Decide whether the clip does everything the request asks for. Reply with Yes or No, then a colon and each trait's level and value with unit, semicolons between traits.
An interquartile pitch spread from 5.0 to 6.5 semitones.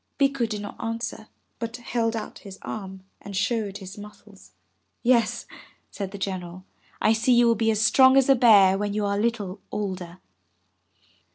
No: average, 2.9 semitones